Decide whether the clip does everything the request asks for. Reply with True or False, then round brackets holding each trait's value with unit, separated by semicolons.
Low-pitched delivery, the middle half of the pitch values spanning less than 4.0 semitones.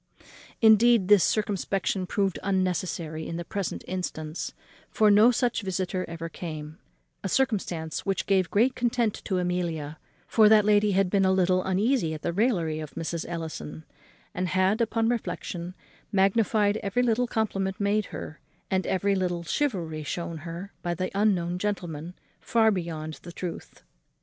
False (190 Hz; 3.6 semitones)